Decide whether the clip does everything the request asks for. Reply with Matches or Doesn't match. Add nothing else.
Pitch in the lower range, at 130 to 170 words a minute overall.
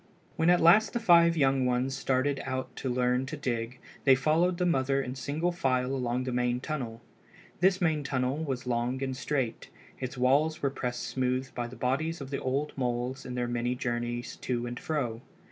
Doesn't match